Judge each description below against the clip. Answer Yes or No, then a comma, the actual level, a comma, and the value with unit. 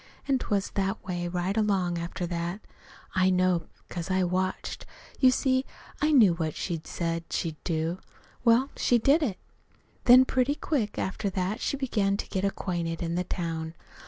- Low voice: No, medium, 185 Hz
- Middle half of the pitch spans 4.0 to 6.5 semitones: Yes, average, 5.0 semitones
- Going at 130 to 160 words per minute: No, average, 170 wpm